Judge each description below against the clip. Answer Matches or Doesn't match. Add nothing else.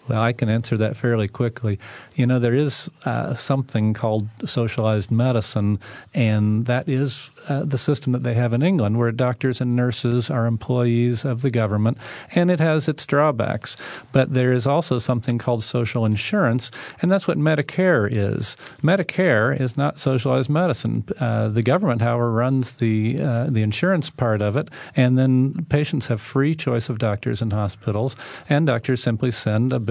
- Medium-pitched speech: Doesn't match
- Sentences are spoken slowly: Doesn't match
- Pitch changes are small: Doesn't match